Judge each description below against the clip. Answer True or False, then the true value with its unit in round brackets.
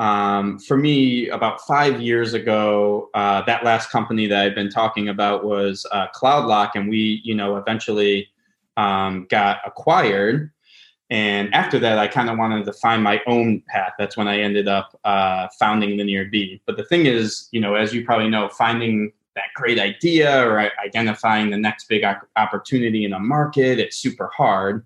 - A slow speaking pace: False (175 wpm)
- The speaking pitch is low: True (105 Hz)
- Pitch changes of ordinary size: False (2.1 semitones)